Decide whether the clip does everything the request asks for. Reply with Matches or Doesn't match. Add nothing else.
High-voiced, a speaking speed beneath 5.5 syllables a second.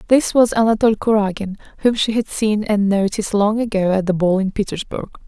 Doesn't match